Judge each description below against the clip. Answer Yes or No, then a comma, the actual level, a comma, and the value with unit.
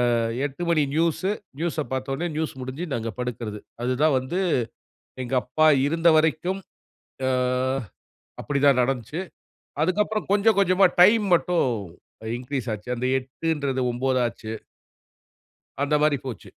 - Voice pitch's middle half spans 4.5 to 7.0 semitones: Yes, average, 4.8 semitones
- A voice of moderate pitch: Yes, medium, 145 Hz